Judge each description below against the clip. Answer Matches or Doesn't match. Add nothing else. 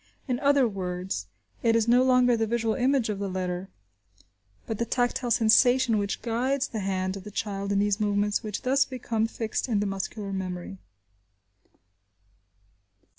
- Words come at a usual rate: Matches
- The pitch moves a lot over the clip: Doesn't match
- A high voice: Matches